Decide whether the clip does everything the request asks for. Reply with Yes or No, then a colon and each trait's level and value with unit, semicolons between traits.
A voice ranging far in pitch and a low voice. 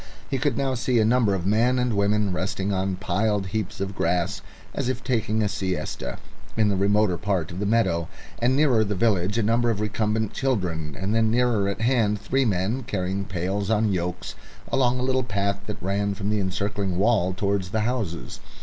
No: average, 3.1 semitones; low, 105 Hz